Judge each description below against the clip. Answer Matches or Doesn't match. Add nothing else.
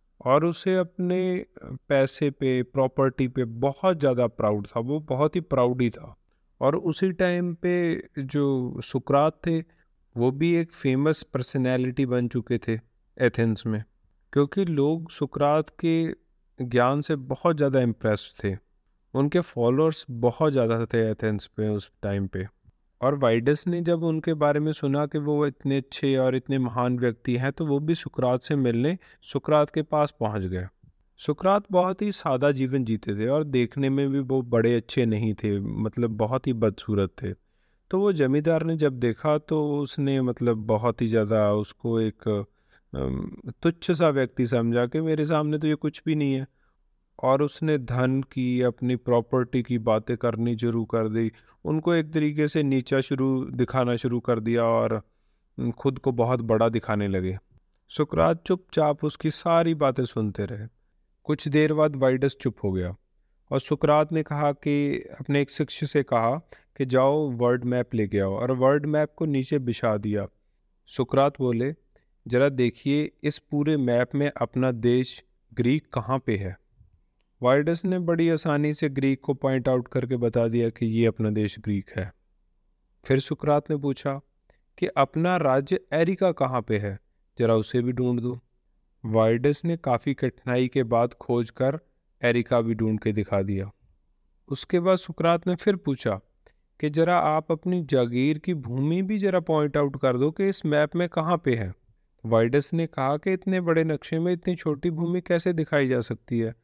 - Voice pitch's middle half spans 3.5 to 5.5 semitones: Matches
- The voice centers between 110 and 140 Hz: Matches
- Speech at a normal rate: Matches